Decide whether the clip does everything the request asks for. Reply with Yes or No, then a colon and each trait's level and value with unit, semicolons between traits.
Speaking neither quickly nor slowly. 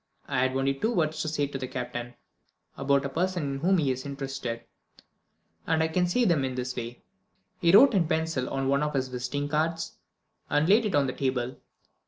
No: fast, 210 wpm